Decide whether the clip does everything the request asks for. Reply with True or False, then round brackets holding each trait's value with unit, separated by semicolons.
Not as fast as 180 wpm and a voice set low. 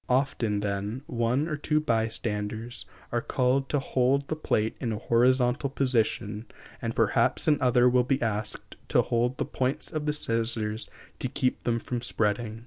True (160 wpm; 120 Hz)